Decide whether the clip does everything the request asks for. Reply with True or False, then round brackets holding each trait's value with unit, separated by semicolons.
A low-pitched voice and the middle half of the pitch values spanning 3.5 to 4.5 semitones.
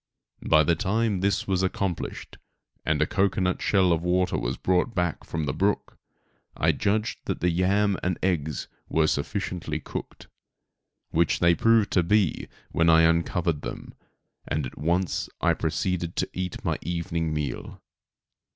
False (90 Hz; 2.7 semitones)